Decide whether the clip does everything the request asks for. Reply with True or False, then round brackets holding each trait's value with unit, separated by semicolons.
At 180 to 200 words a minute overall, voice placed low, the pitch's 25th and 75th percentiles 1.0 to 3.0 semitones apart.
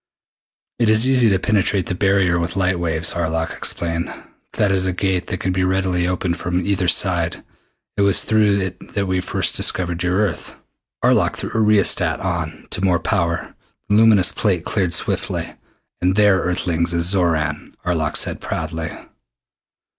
False (165 wpm; 90 Hz; 2.5 semitones)